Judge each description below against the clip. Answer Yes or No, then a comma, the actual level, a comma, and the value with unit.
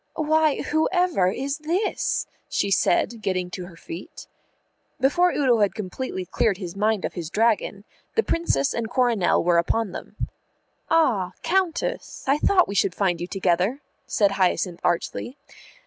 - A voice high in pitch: Yes, high, 215 Hz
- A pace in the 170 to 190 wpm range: No, average, 145 wpm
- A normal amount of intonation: No, wide, 8.3 semitones